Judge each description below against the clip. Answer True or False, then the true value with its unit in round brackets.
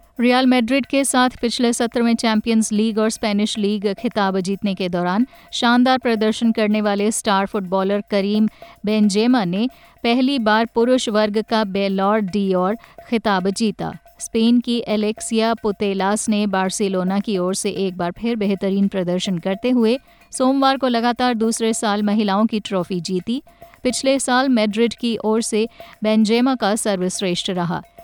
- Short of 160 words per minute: True (150 wpm)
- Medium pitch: False (220 Hz)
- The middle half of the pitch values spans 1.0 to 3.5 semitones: True (3.1 semitones)